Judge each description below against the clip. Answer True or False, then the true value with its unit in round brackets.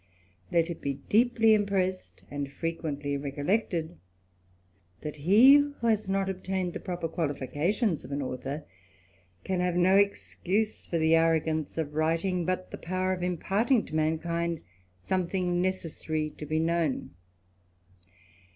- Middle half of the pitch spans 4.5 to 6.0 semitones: False (3.4 semitones)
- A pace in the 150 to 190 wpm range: False (135 wpm)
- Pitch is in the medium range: True (170 Hz)